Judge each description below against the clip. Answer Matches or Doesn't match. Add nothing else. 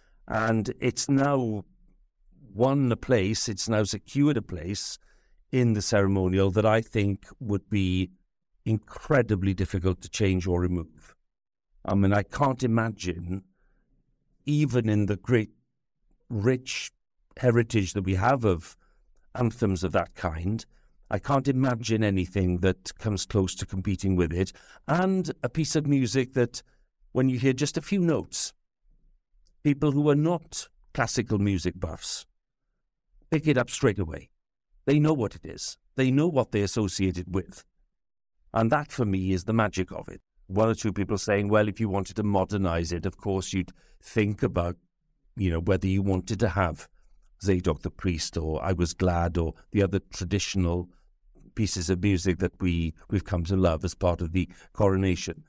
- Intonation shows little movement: Doesn't match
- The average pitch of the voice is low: Matches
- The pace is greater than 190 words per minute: Doesn't match